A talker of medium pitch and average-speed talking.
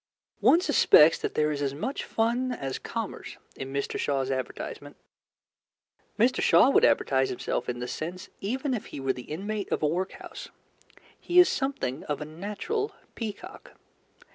Yes: medium, 175 Hz; average, 160 wpm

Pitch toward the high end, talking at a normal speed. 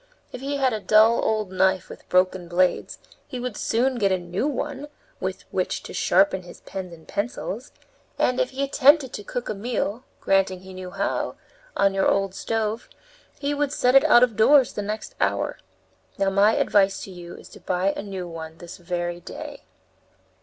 Yes: high, 200 Hz; average, 190 wpm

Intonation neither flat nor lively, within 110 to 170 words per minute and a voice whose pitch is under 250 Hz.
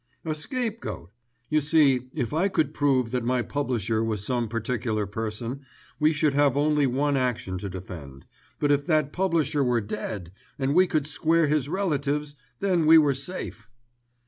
Yes: average, 4.9 semitones; average, 165 wpm; medium, 140 Hz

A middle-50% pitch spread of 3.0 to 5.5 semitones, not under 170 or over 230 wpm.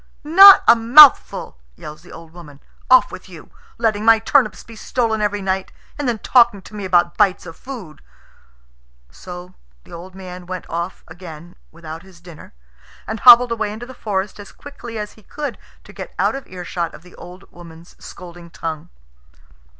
Yes: average, 4.8 semitones; average, 175 wpm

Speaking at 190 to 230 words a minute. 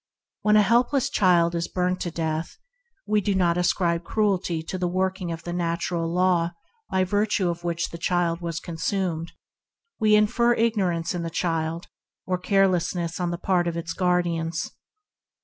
No: average, 165 wpm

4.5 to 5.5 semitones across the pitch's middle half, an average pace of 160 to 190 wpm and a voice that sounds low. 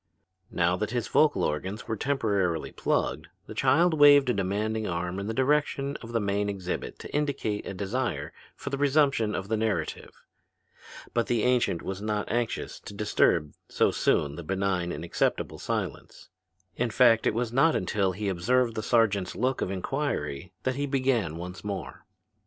Yes: average, 5.0 semitones; average, 170 wpm; low, 105 Hz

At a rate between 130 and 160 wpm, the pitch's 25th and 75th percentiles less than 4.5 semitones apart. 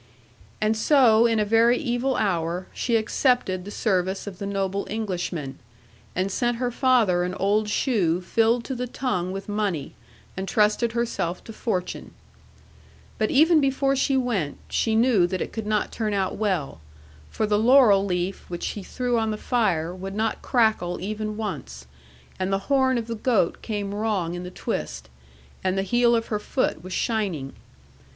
No: average, 175 wpm; average, 4.1 semitones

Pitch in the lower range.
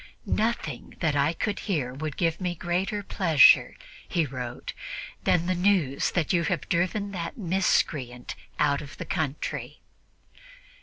No: medium, 165 Hz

